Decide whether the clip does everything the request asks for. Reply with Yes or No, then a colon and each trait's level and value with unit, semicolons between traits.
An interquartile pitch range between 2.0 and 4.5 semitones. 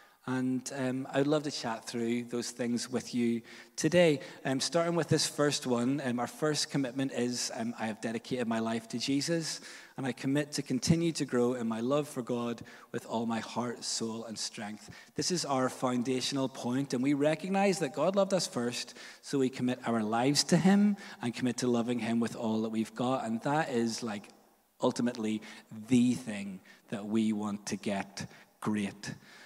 Yes: average, 3.8 semitones